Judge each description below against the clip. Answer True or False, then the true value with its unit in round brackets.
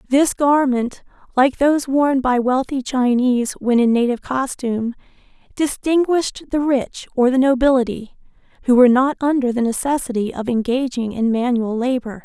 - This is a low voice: False (255 Hz)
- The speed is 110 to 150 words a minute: True (140 wpm)